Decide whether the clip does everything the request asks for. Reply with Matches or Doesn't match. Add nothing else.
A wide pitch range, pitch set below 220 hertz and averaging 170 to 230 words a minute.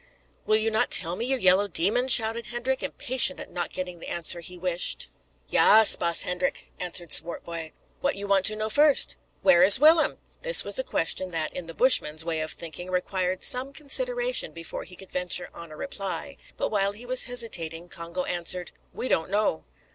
Matches